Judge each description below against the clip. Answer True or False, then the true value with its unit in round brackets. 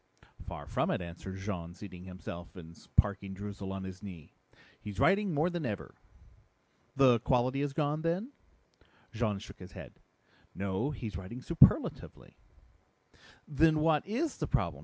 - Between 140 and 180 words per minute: True (145 wpm)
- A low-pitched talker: True (105 Hz)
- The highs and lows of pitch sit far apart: True (7.9 semitones)